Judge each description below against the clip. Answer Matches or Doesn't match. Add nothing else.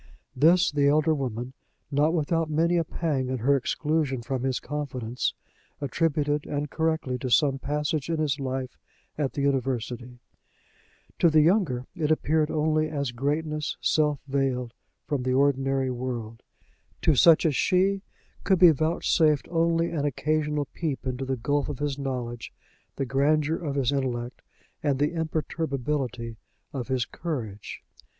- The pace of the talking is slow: Doesn't match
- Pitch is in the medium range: Matches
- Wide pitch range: Doesn't match